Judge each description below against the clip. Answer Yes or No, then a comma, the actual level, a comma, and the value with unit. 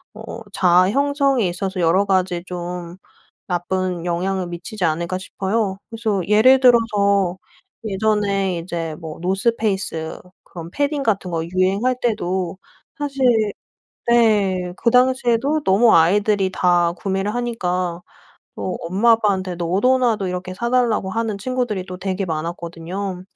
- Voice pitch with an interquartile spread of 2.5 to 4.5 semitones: Yes, average, 4.1 semitones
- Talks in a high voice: Yes, high, 195 Hz